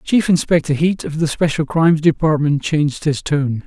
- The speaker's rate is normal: Yes, average, 180 wpm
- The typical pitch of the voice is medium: Yes, medium, 155 Hz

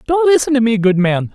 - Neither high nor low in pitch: No, high, 225 Hz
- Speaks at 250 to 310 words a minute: Yes, fast, 270 wpm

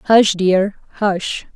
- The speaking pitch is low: No, high, 195 Hz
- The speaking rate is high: No, slow, 115 wpm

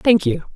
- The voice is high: Yes, high, 210 Hz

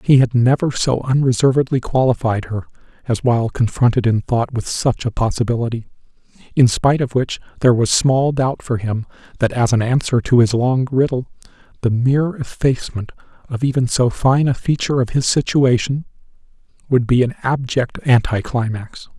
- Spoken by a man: Yes, male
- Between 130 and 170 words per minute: Yes, average, 160 wpm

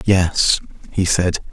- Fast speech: No, slow, 120 wpm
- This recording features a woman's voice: No, male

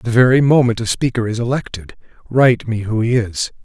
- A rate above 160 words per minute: Yes, average, 200 wpm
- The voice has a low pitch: Yes, low, 120 Hz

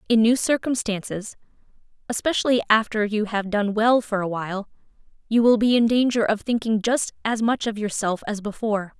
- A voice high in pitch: Yes, high, 220 Hz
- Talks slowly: No, average, 175 wpm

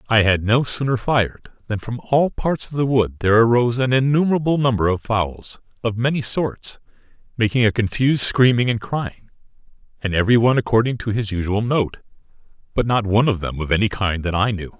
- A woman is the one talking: No, male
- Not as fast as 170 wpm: No, average, 190 wpm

